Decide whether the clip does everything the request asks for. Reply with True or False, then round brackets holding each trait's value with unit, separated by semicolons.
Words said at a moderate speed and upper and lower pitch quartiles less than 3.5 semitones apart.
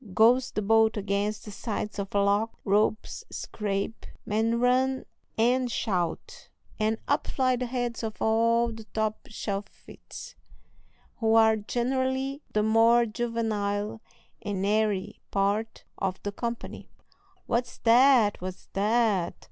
False (125 wpm; 2.5 semitones)